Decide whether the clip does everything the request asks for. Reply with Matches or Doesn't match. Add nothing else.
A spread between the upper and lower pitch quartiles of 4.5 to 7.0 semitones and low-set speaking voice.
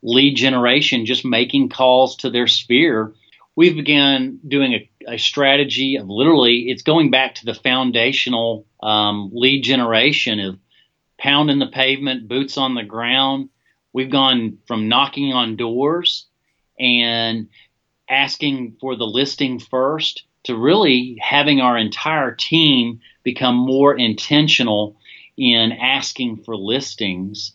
Doesn't match